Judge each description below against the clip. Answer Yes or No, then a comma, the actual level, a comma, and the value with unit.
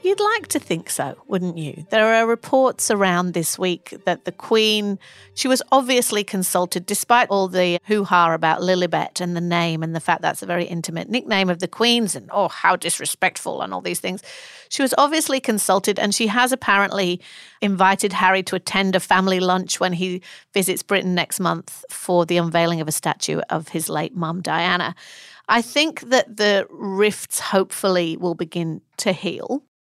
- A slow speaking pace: No, average, 185 wpm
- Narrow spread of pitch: No, average, 3.8 semitones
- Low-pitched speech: No, high, 190 Hz